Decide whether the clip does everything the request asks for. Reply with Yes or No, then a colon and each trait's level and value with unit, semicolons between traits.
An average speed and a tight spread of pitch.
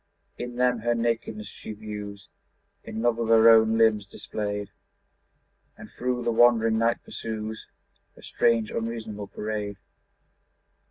No: slow, 125 wpm; narrow, 1.6 semitones